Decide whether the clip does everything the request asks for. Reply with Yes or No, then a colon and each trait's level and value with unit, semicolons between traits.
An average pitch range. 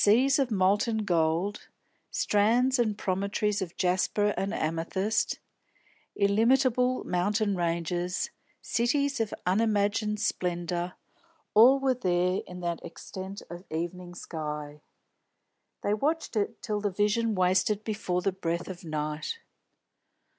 Yes: average, 3.7 semitones